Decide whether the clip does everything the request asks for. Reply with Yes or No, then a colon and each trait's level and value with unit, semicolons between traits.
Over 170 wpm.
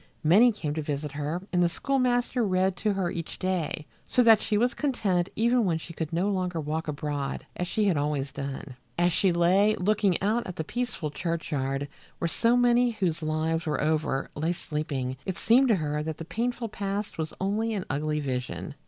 Yes: average, 195 wpm